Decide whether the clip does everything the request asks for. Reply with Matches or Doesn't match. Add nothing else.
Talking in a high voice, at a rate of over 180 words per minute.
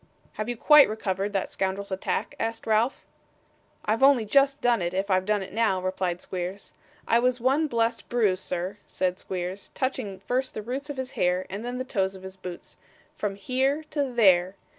Matches